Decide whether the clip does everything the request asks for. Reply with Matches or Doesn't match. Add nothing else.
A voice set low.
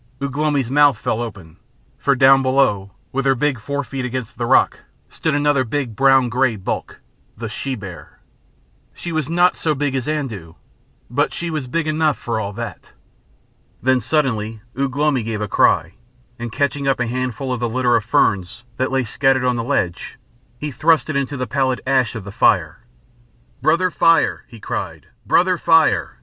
Matches